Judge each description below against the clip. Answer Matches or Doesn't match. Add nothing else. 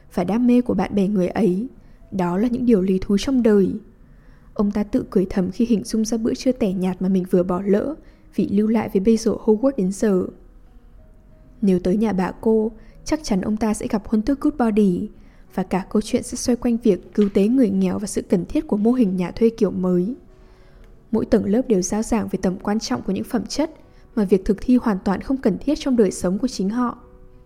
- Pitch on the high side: Matches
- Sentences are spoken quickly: Matches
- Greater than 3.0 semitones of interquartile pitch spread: Matches